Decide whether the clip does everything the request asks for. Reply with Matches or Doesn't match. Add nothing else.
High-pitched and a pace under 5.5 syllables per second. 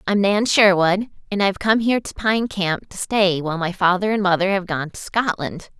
Matches